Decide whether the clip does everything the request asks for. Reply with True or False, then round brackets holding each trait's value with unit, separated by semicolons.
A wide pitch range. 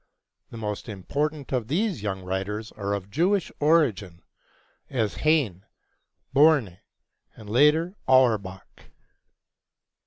True (7.1 semitones)